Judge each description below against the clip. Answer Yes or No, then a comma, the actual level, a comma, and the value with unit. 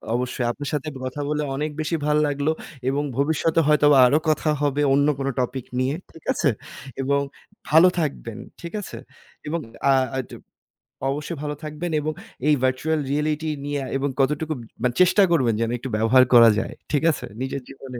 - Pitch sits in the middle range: Yes, medium, 145 Hz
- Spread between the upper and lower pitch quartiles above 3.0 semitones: No, narrow, 2.4 semitones